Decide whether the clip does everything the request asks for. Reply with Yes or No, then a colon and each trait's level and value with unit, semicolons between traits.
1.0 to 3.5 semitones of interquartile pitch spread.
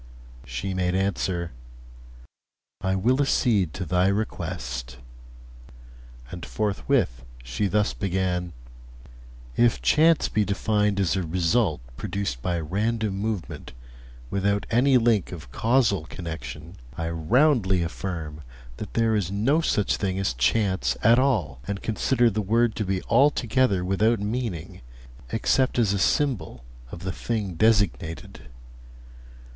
No: average, 4.5 semitones